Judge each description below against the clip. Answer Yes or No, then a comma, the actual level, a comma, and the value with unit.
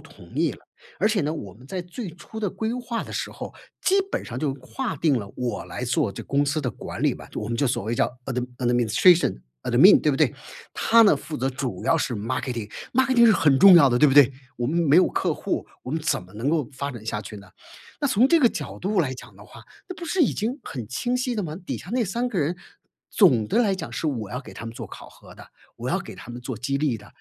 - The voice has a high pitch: No, medium, 145 Hz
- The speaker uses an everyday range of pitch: No, wide, 8.9 semitones